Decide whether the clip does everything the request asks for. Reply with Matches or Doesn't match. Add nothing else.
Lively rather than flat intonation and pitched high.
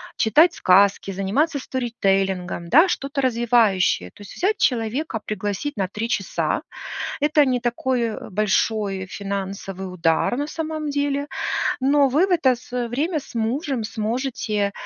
Matches